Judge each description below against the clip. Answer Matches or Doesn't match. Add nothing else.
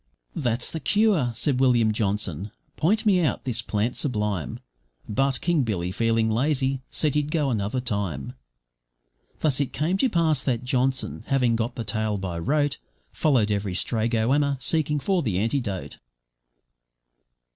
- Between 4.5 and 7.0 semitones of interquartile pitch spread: Matches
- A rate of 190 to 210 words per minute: Doesn't match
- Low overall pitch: Matches